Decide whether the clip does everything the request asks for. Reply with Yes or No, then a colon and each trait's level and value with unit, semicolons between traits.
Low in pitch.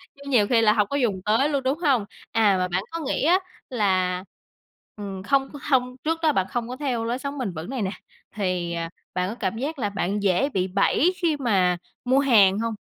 No: high, 225 Hz